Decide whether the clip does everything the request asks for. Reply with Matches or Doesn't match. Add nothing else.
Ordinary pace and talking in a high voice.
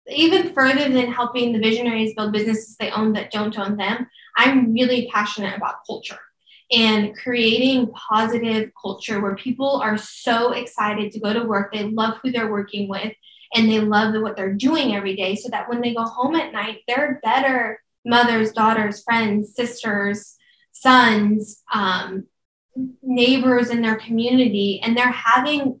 Matches